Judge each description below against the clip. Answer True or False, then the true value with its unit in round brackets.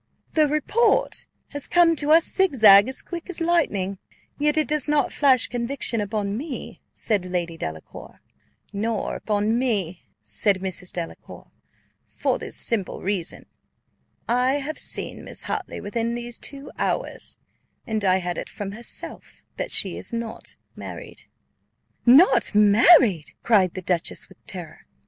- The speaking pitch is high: True (230 Hz)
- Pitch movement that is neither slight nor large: False (6.6 semitones)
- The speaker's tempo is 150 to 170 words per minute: False (140 wpm)